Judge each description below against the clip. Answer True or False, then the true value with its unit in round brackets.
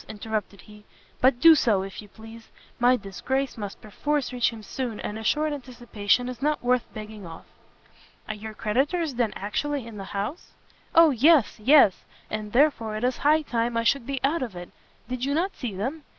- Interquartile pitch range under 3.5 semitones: False (4.6 semitones)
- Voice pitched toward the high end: True (240 Hz)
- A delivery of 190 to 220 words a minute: True (195 wpm)